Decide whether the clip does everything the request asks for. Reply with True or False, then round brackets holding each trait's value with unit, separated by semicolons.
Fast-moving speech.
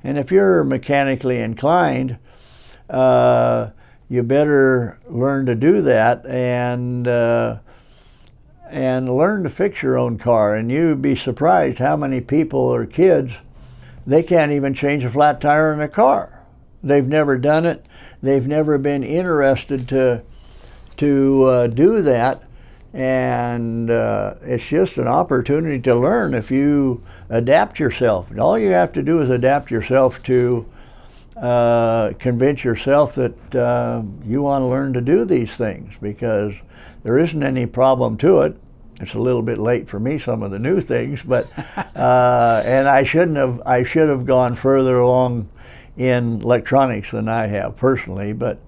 False (155 wpm)